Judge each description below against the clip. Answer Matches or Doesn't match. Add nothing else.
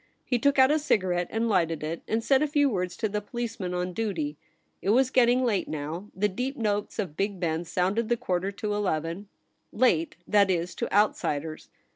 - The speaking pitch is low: Doesn't match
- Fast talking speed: Matches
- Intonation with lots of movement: Doesn't match